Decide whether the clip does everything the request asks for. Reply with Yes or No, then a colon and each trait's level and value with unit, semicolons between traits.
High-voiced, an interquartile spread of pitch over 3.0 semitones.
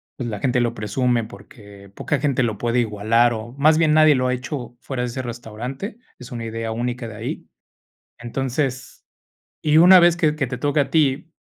No: low, 125 Hz; average, 3.6 semitones